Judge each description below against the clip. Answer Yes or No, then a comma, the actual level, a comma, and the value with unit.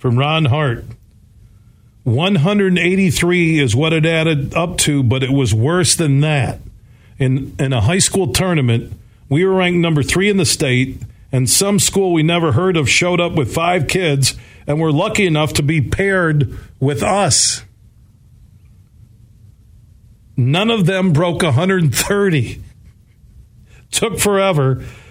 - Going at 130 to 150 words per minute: Yes, average, 140 wpm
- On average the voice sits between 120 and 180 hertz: Yes, medium, 140 Hz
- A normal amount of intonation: No, wide, 7.0 semitones